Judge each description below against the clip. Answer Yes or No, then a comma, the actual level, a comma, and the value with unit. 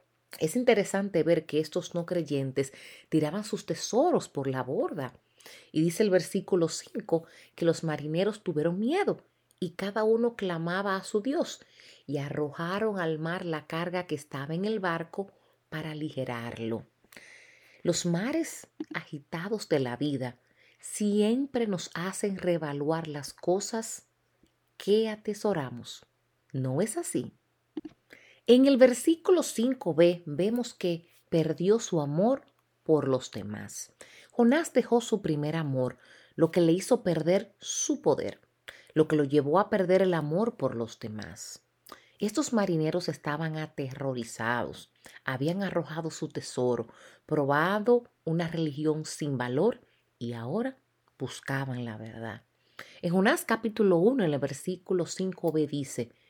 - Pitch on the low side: No, medium, 170 Hz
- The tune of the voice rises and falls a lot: Yes, wide, 6.0 semitones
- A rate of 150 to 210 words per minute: No, average, 130 wpm